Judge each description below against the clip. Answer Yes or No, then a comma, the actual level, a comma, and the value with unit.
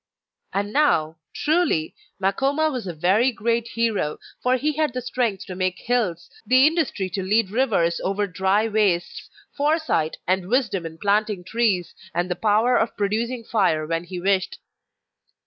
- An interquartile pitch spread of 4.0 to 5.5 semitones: Yes, average, 5.2 semitones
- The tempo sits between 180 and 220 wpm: No, average, 155 wpm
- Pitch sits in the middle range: No, high, 210 Hz